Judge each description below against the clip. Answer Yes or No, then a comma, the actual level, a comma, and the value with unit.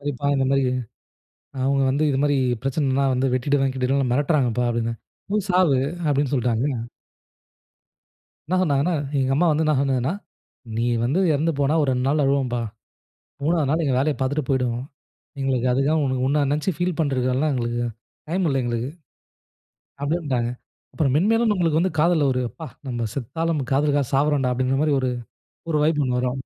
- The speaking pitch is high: No, medium, 140 Hz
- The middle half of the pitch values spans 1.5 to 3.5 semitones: Yes, average, 3.2 semitones